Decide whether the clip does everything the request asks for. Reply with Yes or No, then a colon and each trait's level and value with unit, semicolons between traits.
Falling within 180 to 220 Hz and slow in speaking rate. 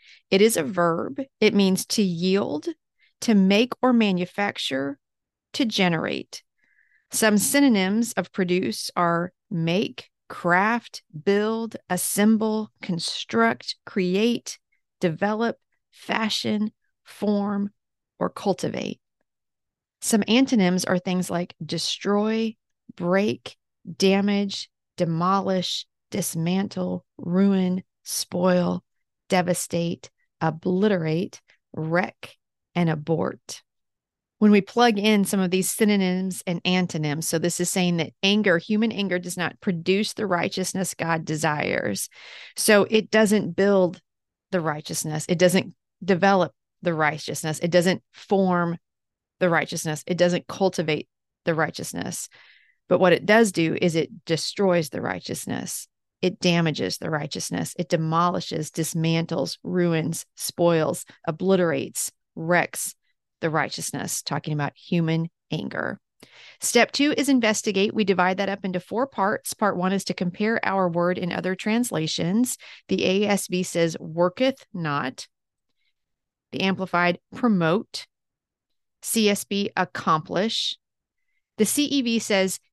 Yes: medium, 185 Hz; slow, 110 wpm